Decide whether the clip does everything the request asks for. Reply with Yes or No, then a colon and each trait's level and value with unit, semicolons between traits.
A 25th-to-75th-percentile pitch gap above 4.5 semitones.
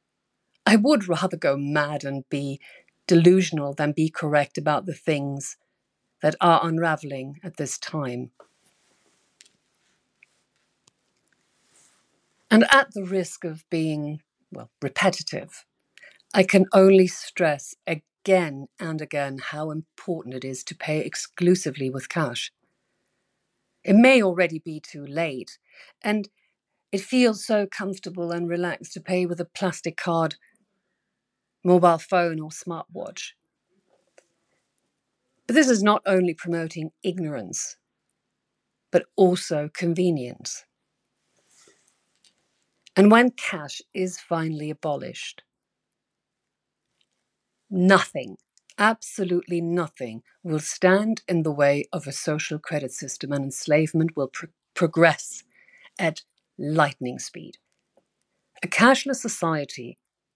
No: average, 4.0 semitones